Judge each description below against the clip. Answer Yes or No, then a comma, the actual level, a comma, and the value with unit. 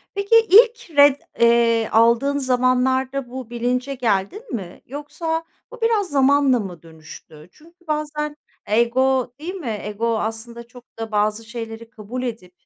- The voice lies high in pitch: Yes, very high, 250 Hz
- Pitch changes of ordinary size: Yes, average, 4.3 semitones